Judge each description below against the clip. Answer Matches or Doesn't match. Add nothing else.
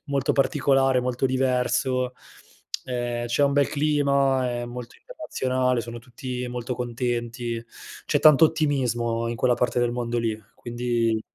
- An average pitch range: Doesn't match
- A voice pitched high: Doesn't match